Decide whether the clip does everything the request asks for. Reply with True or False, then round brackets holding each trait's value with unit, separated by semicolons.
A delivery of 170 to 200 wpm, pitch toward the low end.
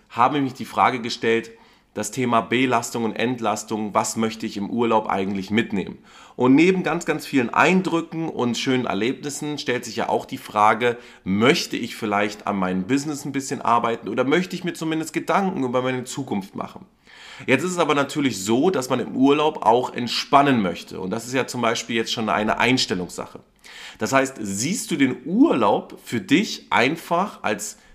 True (185 wpm; 125 Hz)